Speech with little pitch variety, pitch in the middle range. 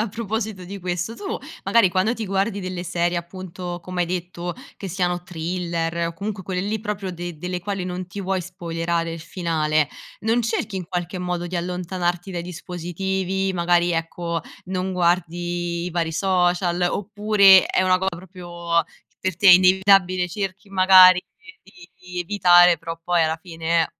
Yes: narrow, 1.7 semitones; medium, 180 Hz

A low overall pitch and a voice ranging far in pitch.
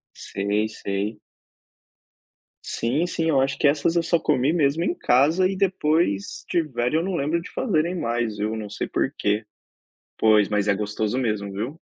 Yes: low, 130 Hz; wide, 7.6 semitones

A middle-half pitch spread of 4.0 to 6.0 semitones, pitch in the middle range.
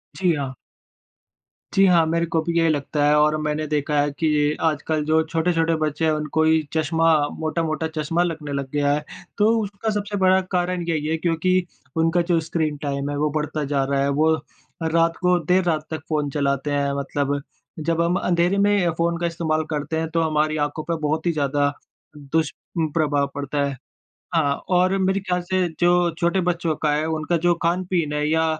No: narrow, 2.5 semitones; medium, 160 Hz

